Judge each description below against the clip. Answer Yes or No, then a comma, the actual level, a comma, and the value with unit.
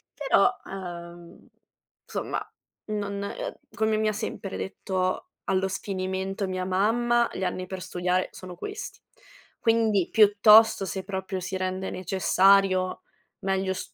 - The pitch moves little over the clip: Yes, narrow, 2.3 semitones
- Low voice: No, high, 190 Hz